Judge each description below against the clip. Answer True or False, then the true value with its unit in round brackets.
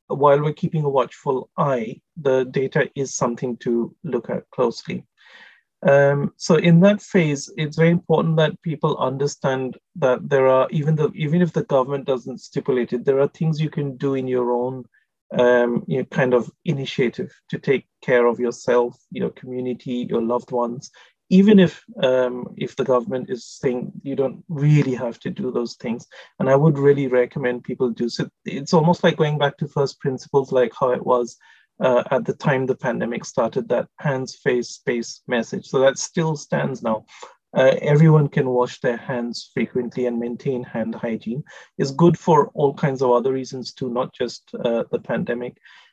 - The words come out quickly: False (185 wpm)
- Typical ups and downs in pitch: True (4.0 semitones)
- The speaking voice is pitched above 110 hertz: True (135 Hz)